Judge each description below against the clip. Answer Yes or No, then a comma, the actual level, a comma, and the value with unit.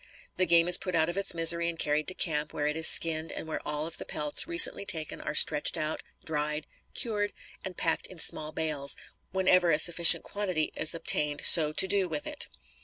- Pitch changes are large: No, average, 2.9 semitones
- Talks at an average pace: No, fast, 210 wpm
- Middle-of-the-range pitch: Yes, medium, 160 Hz